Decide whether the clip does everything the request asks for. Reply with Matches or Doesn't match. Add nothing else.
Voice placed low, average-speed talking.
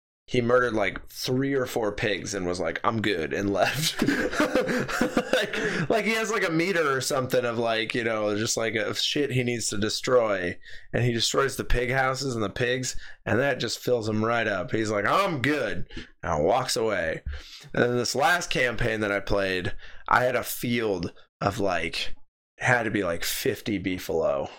Matches